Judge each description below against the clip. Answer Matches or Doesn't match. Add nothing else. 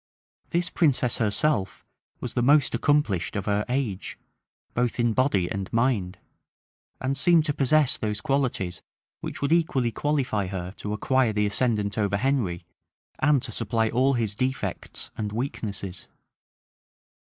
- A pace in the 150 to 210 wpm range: Doesn't match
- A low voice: Matches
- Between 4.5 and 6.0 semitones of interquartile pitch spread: Matches